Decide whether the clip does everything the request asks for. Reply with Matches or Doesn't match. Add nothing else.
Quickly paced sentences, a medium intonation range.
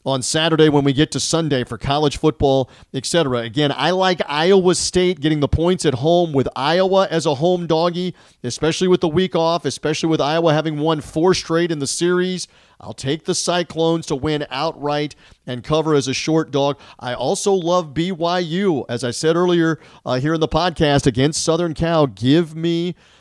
Doesn't match